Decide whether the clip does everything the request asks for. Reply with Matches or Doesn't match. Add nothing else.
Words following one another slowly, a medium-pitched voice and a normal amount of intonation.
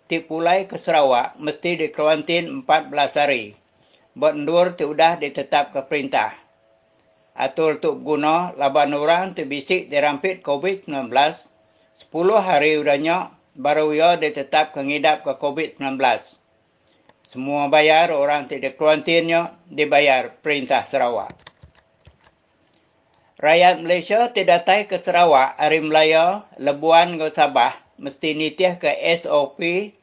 Matches